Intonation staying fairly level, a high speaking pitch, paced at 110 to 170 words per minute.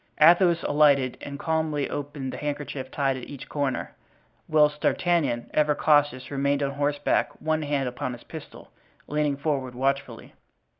No: narrow, 1.8 semitones; medium, 145 Hz; average, 145 wpm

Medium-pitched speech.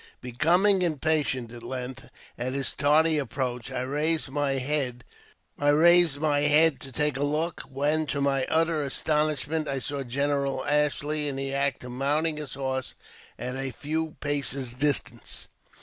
Yes: medium, 145 Hz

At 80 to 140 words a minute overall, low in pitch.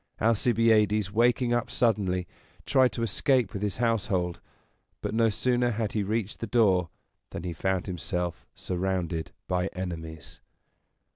Yes: slow, 135 wpm; low, 105 Hz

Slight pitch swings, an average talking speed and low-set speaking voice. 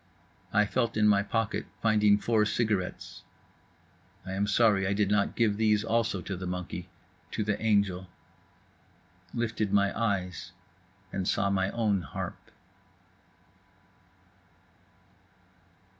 No: narrow, 2.2 semitones; slow, 115 wpm; low, 100 Hz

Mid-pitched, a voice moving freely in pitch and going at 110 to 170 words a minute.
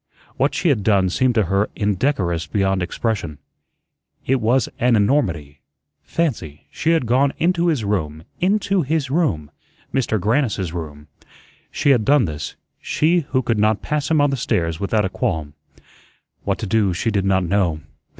No: low, 110 Hz; wide, 7.9 semitones; average, 165 wpm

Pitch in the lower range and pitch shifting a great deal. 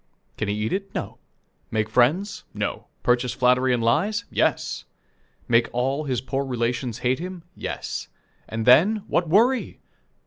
Yes: low, 130 Hz; wide, 7.1 semitones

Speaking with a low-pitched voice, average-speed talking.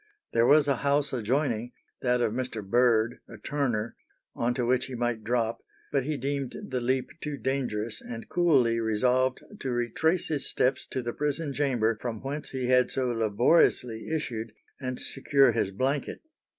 Yes: low, 125 Hz; average, 165 wpm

